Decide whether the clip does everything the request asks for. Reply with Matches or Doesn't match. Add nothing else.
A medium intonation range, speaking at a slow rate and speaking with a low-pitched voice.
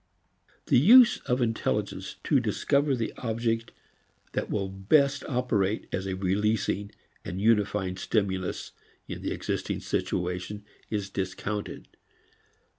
Matches